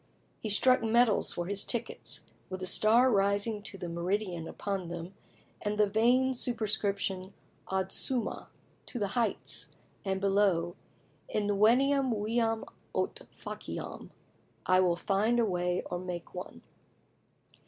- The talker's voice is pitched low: No, high, 205 Hz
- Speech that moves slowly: Yes, slow, 130 wpm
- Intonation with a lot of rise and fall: No, average, 3.5 semitones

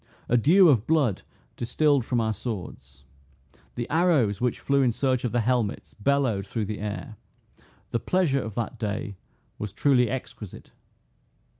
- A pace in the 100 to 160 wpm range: Yes, average, 150 wpm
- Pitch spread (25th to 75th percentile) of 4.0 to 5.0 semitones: Yes, average, 4.5 semitones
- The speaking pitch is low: Yes, low, 120 Hz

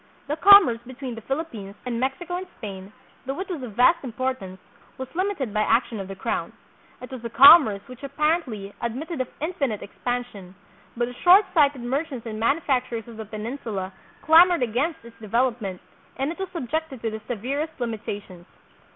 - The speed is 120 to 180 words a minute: Yes, average, 175 wpm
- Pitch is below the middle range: No, very high, 250 Hz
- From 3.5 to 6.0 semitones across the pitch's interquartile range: Yes, wide, 5.6 semitones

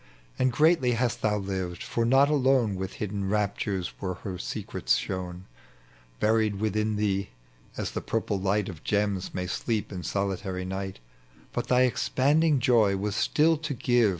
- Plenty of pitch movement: No, average, 4.2 semitones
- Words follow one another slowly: No, average, 160 wpm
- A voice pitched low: Yes, low, 105 Hz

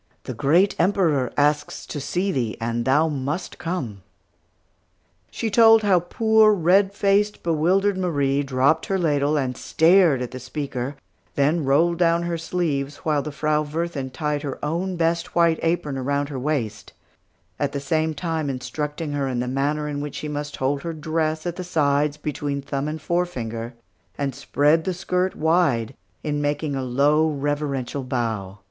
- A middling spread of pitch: Yes, average, 3.6 semitones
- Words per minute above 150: Yes, average, 165 wpm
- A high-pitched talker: No, medium, 150 Hz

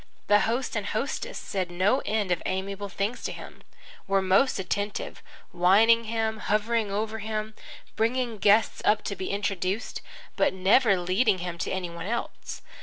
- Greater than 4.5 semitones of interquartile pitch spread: No, average, 2.8 semitones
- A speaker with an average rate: Yes, average, 160 wpm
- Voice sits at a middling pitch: No, high, 205 Hz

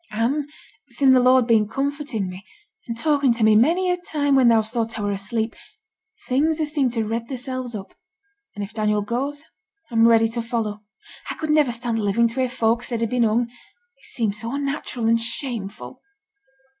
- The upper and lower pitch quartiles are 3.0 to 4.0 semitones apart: Yes, average, 3.6 semitones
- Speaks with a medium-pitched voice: No, high, 235 Hz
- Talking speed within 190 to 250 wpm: Yes, average, 195 wpm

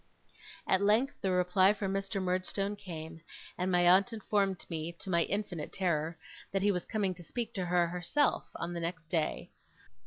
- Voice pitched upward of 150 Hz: Yes, medium, 185 Hz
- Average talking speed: Yes, average, 180 wpm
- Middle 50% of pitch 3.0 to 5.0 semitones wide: No, narrow, 2.5 semitones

